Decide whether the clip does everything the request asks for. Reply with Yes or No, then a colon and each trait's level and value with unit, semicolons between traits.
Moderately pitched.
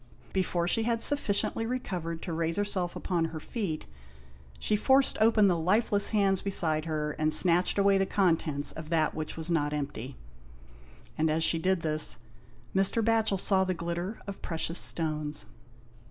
Yes: medium, 175 Hz